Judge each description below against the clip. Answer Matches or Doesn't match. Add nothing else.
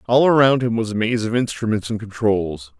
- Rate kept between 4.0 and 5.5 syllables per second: Matches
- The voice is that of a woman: Doesn't match